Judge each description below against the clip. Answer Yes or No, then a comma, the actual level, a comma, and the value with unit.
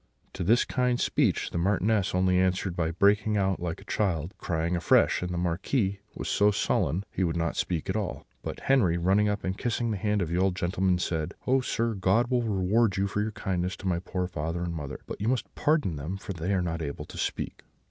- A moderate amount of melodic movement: Yes, average, 3.2 semitones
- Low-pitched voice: Yes, very low, 95 Hz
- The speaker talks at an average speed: No, fast, 230 wpm